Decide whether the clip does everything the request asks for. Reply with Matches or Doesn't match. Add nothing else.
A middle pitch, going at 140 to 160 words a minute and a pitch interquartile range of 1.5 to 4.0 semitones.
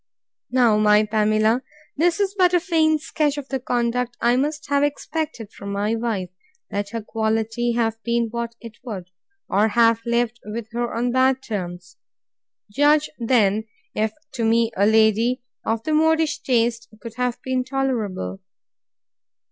Doesn't match